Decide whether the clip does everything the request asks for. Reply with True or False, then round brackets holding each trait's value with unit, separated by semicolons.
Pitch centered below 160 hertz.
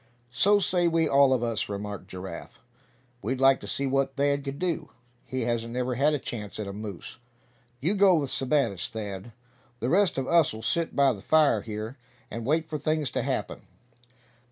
True (135 Hz)